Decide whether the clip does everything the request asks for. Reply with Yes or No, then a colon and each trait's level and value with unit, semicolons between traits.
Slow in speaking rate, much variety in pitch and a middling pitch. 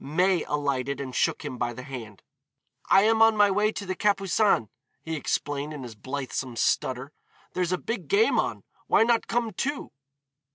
No: average, 175 wpm; wide, 8.0 semitones; medium, 160 Hz